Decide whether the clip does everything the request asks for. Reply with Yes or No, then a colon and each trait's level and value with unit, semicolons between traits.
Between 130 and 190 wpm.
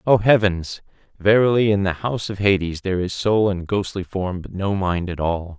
No: fast, 205 wpm